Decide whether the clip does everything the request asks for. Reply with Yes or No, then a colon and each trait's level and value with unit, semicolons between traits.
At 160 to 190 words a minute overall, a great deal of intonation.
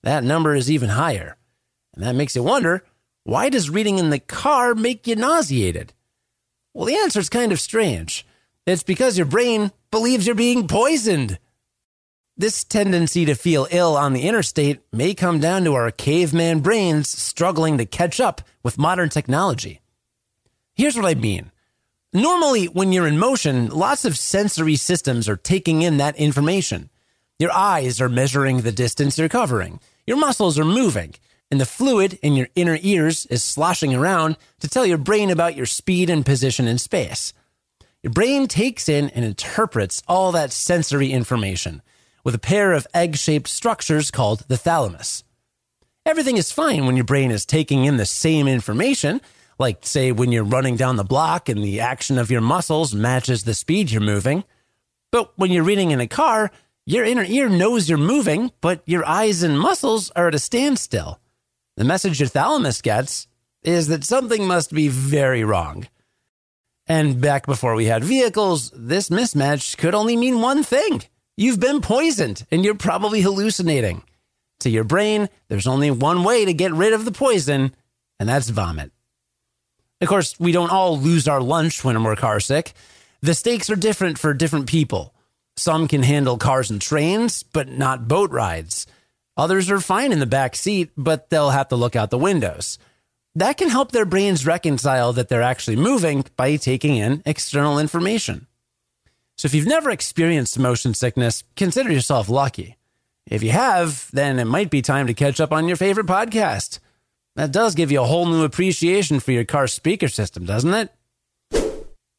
Yes: average, 175 wpm; wide, 7.1 semitones